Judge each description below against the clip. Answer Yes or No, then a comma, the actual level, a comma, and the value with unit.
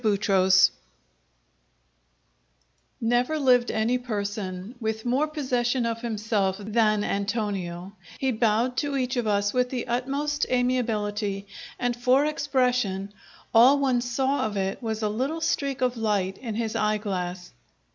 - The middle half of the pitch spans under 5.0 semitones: Yes, average, 3.6 semitones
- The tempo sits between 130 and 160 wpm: Yes, slow, 135 wpm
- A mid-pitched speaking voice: No, high, 230 Hz